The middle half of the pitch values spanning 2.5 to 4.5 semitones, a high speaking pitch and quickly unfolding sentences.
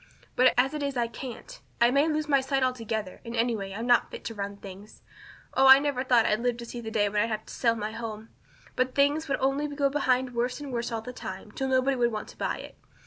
Yes: average, 3.3 semitones; high, 245 Hz; fast, 260 wpm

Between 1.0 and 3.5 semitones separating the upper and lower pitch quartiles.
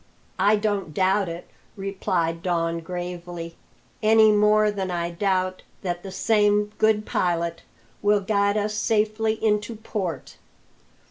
Yes: average, 3.1 semitones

